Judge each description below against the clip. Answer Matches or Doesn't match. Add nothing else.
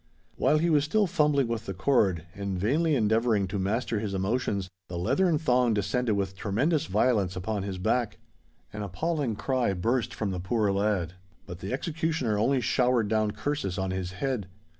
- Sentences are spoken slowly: Doesn't match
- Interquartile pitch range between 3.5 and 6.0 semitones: Matches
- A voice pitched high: Doesn't match